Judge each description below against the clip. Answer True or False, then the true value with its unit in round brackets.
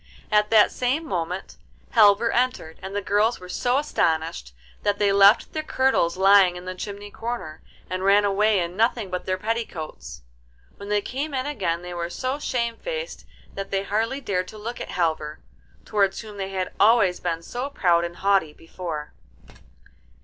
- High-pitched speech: True (200 Hz)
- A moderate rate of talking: True (170 wpm)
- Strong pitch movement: False (4.3 semitones)